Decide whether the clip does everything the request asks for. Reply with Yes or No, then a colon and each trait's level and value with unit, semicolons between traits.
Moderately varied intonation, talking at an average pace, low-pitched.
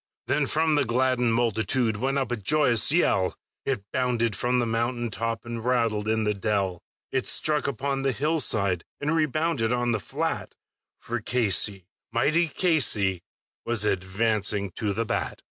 Yes: average, 4.1 semitones; average, 155 wpm; low, 120 Hz